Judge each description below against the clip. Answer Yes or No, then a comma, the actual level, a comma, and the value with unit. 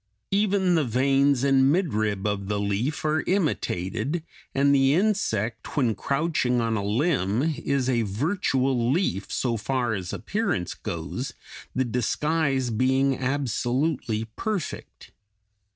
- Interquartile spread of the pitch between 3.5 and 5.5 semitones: Yes, average, 5.2 semitones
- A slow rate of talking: Yes, slow, 120 wpm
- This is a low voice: Yes, low, 130 Hz